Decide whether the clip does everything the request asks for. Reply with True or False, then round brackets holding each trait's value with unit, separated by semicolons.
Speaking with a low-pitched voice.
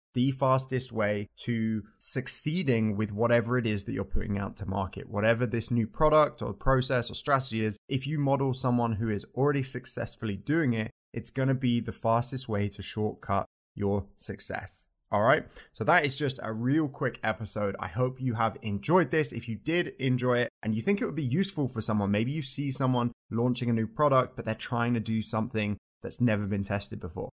True (120 Hz)